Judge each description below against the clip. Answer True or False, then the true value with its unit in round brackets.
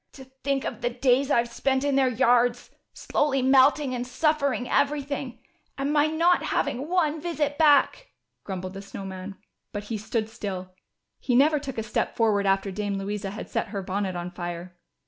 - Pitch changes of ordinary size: False (5.9 semitones)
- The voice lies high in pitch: True (245 Hz)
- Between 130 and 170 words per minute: False (185 wpm)